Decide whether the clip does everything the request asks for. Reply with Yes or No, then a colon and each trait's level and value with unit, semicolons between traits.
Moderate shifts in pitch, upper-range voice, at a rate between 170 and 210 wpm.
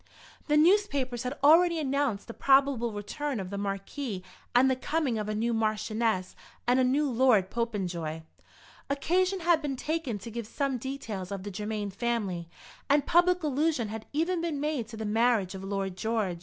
No: wide, 5.8 semitones; high, 240 Hz; average, 175 wpm